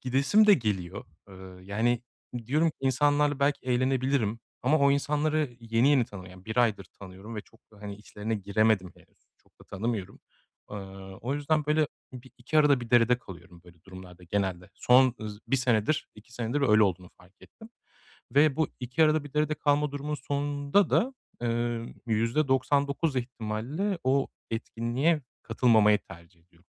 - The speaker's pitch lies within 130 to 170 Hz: No, low, 120 Hz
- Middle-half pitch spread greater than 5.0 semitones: Yes, wide, 5.6 semitones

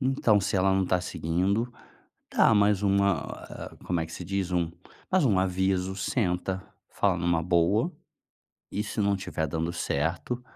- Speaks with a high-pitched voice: No, very low, 95 Hz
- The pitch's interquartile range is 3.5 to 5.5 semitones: No, average, 2.7 semitones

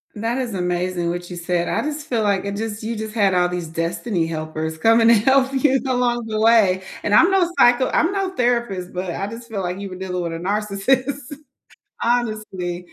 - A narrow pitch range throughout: No, average, 5.1 semitones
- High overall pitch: Yes, high, 210 Hz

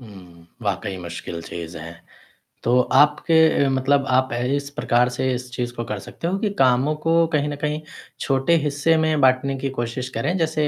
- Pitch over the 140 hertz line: No, low, 130 Hz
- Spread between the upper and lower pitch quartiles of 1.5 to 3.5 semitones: No, average, 3.9 semitones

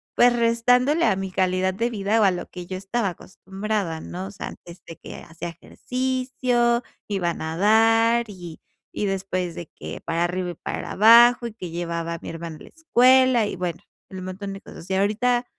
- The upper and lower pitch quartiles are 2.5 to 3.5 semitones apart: No, average, 4.9 semitones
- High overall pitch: Yes, high, 195 Hz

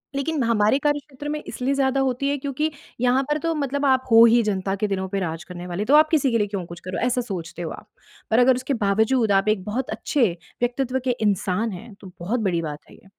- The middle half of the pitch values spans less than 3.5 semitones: No, wide, 5.5 semitones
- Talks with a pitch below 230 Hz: No, high, 235 Hz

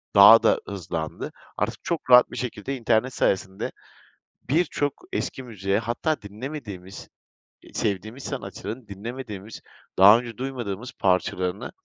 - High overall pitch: No, low, 110 Hz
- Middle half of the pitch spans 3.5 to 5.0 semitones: Yes, average, 4.5 semitones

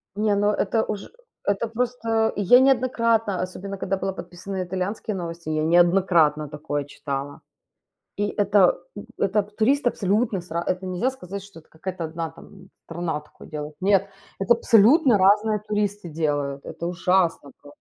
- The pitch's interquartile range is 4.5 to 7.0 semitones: No, average, 3.9 semitones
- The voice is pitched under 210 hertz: Yes, high, 190 Hz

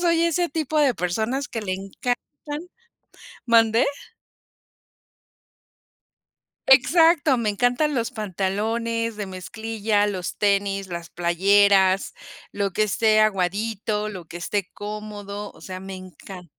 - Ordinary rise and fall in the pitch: Yes, average, 3.4 semitones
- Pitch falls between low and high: No, high, 210 Hz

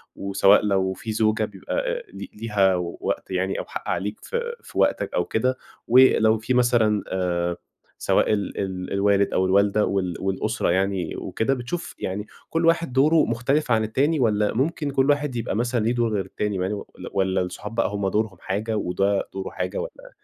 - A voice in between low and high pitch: No, low, 105 Hz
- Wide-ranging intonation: No, average, 4.2 semitones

